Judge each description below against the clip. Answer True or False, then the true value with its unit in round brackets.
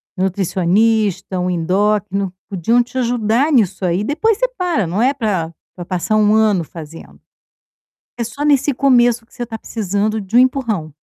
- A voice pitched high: True (215 Hz)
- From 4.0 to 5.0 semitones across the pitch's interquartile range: True (4.6 semitones)